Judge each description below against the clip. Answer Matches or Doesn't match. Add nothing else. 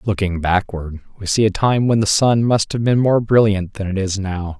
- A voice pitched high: Doesn't match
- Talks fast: Matches